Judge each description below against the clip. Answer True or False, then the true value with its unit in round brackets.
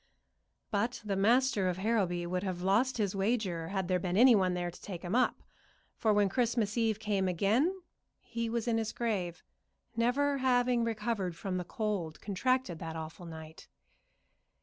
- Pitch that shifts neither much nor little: True (4.4 semitones)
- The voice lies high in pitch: True (205 Hz)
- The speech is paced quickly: False (165 wpm)